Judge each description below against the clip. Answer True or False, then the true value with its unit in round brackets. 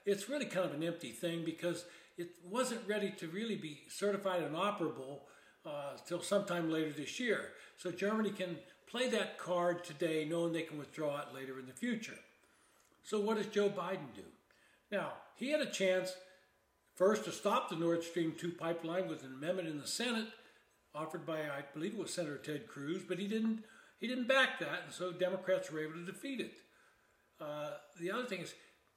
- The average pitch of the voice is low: False (180 Hz)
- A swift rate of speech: False (195 wpm)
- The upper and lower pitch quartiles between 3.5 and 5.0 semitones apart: True (4.0 semitones)